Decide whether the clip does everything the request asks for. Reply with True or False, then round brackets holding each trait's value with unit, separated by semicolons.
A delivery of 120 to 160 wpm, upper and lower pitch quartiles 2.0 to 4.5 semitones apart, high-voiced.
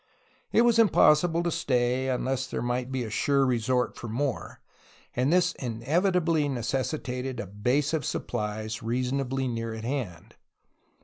False (140 wpm; 3.5 semitones; 130 Hz)